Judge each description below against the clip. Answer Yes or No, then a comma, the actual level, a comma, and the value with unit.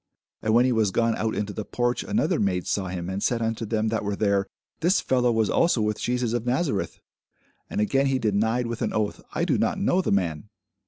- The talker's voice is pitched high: No, low, 110 Hz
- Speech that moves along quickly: Yes, fast, 225 wpm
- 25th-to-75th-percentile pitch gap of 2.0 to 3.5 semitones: Yes, average, 3.1 semitones